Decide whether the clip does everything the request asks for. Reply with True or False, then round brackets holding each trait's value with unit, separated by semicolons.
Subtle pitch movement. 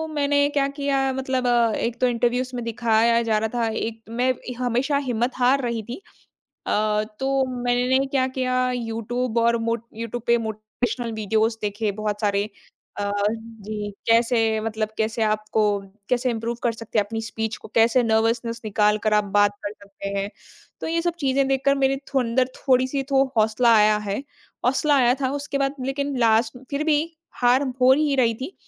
False (3.0 semitones)